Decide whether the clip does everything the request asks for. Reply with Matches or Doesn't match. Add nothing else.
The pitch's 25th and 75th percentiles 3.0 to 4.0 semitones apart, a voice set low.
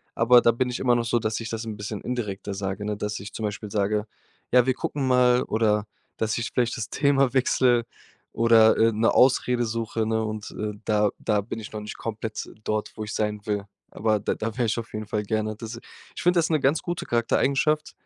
Doesn't match